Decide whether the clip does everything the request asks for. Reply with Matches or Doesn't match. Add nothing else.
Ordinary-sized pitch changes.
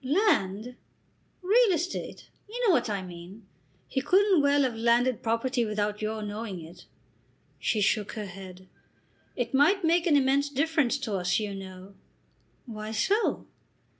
Doesn't match